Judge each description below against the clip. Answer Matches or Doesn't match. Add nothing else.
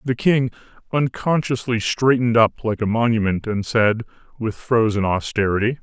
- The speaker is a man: Matches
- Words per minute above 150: Doesn't match